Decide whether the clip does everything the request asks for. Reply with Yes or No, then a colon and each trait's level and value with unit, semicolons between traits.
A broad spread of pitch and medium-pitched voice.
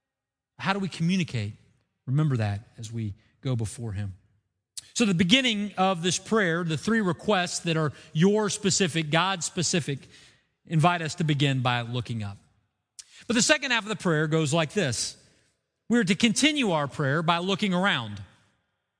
Yes: wide, 8.2 semitones; medium, 160 Hz